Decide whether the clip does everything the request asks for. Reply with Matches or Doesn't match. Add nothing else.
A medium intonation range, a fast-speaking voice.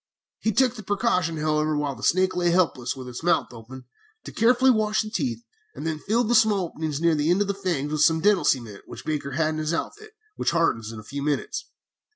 Doesn't match